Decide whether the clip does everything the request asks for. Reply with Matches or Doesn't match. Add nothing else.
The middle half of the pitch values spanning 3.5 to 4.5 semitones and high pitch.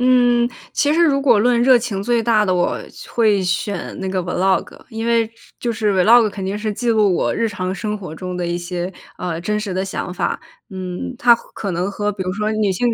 Matches